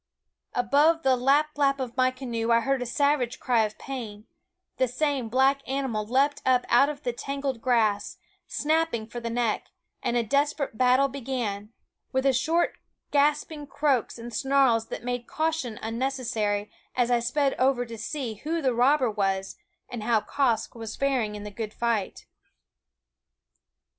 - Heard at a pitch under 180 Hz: No, very high, 250 Hz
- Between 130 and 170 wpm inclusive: Yes, average, 160 wpm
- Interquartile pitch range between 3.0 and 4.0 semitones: Yes, average, 3.3 semitones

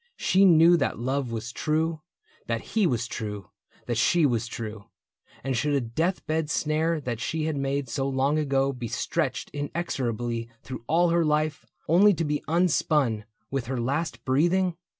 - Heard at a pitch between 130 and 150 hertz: Yes, medium, 140 Hz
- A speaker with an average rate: Yes, average, 170 wpm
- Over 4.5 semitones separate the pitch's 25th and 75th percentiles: Yes, average, 5.0 semitones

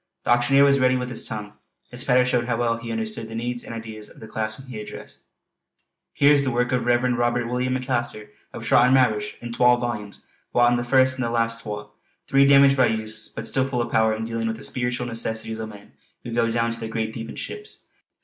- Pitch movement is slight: Yes, narrow, 2.1 semitones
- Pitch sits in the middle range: No, low, 120 Hz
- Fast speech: Yes, fast, 235 wpm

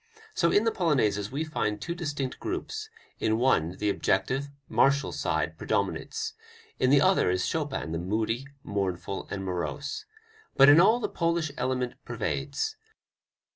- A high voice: No, low, 135 Hz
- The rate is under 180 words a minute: Yes, average, 145 wpm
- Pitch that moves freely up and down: Yes, wide, 8.6 semitones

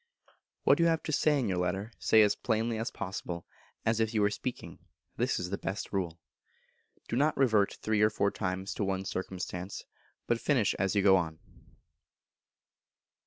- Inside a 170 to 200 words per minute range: Yes, average, 175 wpm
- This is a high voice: No, low, 105 Hz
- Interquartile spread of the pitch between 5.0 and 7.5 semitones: No, average, 3.3 semitones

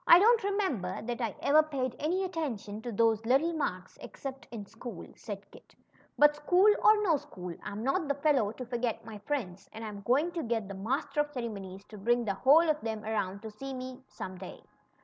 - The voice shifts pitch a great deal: Yes, wide, 6.0 semitones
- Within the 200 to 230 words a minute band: Yes, fast, 205 wpm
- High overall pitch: Yes, high, 240 Hz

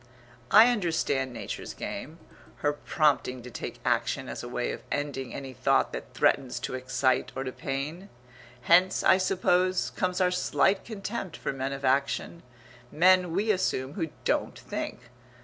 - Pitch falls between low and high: Yes, medium, 145 Hz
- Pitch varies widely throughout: Yes, wide, 5.9 semitones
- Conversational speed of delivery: Yes, average, 155 wpm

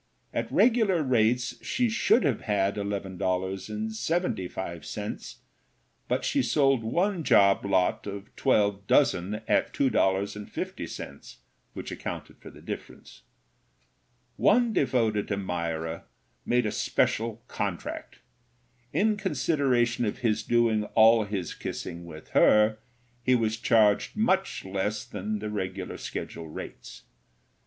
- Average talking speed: No, slow, 110 wpm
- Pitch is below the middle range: Yes, low, 110 Hz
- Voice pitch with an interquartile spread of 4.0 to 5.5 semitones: Yes, average, 4.7 semitones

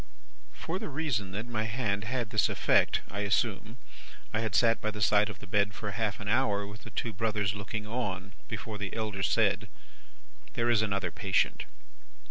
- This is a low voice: Yes, low, 105 Hz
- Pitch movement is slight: Yes, narrow, 2.0 semitones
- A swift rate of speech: No, average, 185 wpm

